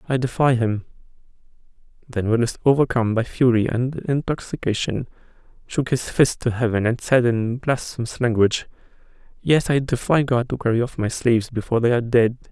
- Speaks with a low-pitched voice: Yes, low, 120 Hz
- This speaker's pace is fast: No, average, 160 wpm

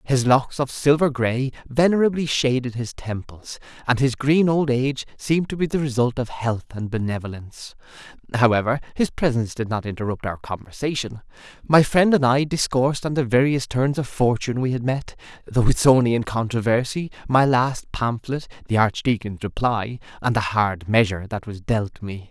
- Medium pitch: No, low, 125 Hz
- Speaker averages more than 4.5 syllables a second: Yes, 5.1 syllables/s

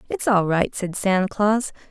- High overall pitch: Yes, high, 205 Hz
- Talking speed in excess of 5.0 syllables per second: No, 4.4 syllables/s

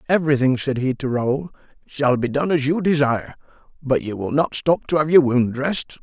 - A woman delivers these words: No, male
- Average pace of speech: No, fast, 210 wpm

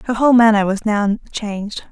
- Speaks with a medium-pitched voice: No, high, 215 Hz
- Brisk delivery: No, average, 190 wpm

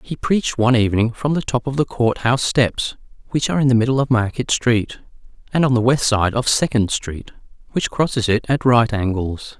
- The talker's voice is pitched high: No, low, 120 Hz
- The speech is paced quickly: Yes, fast, 215 wpm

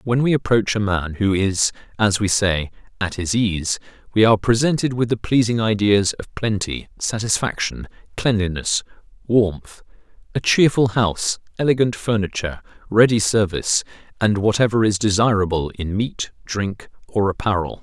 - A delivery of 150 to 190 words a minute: No, average, 140 wpm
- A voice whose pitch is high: No, low, 105 Hz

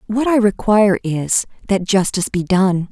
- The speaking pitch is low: No, high, 200 Hz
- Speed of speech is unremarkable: Yes, average, 165 wpm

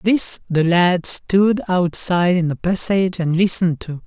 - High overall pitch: No, medium, 180 Hz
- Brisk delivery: No, average, 160 wpm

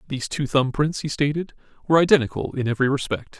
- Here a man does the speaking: Yes, male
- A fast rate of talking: No, average, 195 wpm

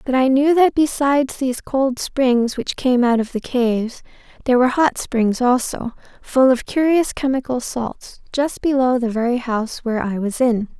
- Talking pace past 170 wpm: Yes, average, 185 wpm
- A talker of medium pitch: No, very high, 255 Hz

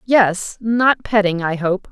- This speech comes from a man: No, female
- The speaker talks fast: No, average, 155 wpm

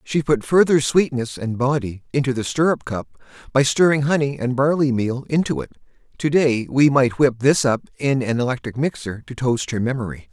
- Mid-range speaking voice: No, low, 130 Hz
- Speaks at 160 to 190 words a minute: Yes, average, 185 wpm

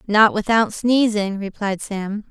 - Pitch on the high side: Yes, high, 210 Hz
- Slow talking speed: Yes, slow, 130 wpm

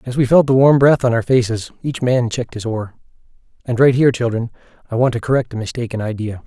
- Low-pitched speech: Yes, low, 120 Hz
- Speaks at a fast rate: Yes, fast, 230 wpm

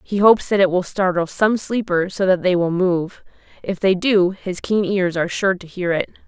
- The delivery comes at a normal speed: No, fast, 230 wpm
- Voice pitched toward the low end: No, medium, 185 Hz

